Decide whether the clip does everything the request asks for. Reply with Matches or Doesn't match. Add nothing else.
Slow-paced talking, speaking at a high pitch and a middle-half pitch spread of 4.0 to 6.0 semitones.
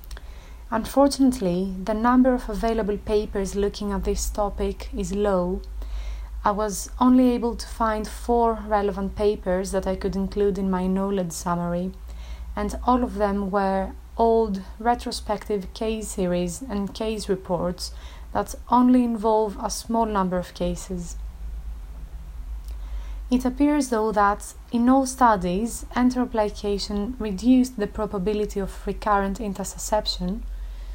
Doesn't match